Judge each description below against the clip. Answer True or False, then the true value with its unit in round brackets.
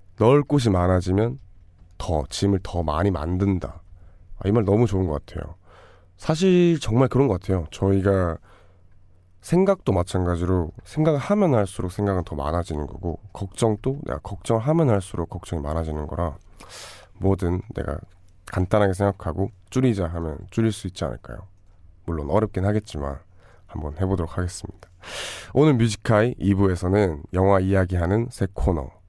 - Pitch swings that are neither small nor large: True (3.1 semitones)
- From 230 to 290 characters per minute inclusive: False (320 characters per minute)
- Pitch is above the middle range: False (95 Hz)